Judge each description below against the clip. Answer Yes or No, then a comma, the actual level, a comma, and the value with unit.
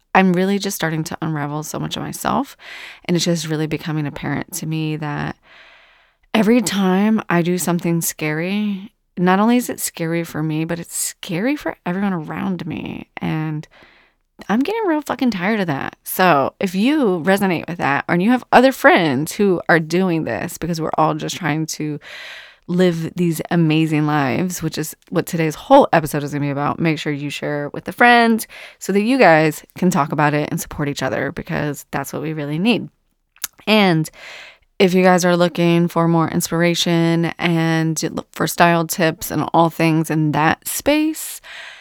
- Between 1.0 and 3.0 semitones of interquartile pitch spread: No, average, 3.8 semitones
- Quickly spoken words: No, average, 185 wpm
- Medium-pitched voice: Yes, medium, 170 Hz